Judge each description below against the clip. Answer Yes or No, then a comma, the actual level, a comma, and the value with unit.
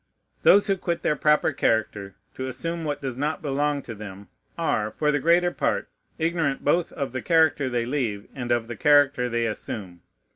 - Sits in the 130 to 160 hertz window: Yes, medium, 140 Hz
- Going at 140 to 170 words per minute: No, average, 185 wpm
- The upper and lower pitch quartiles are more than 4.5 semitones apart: Yes, average, 4.9 semitones